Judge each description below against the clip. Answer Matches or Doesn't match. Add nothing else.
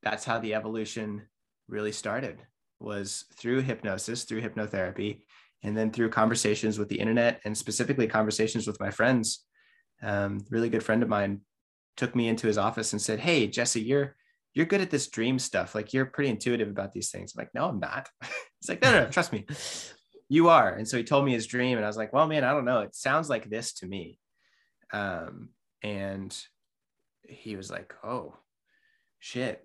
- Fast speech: Doesn't match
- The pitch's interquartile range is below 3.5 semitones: Matches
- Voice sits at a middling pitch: Doesn't match